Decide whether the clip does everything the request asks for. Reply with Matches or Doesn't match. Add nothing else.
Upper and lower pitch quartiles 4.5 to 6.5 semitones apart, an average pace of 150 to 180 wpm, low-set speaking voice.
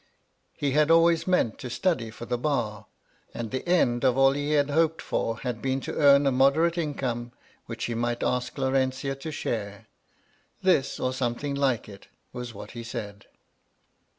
Doesn't match